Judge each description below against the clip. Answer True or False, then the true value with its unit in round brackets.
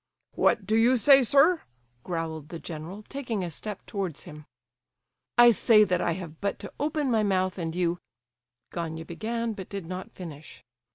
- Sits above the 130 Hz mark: True (190 Hz)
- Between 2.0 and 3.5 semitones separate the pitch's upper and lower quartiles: False (5.3 semitones)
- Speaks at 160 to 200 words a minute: True (170 wpm)